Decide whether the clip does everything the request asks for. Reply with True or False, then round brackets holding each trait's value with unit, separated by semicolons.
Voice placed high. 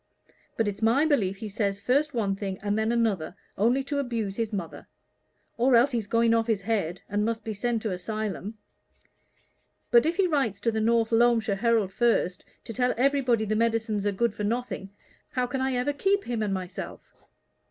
True (225 Hz)